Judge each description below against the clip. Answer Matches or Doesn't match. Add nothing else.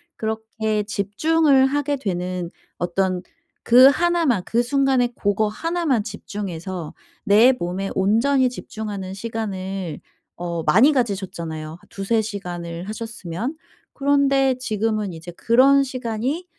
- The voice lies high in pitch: Matches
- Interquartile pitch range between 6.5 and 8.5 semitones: Doesn't match